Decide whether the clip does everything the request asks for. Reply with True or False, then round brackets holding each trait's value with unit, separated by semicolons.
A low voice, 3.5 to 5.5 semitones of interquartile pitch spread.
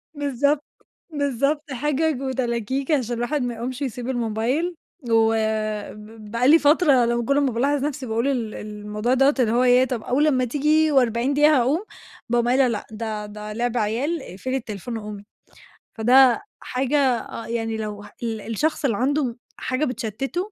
False (250 Hz; 3.8 semitones)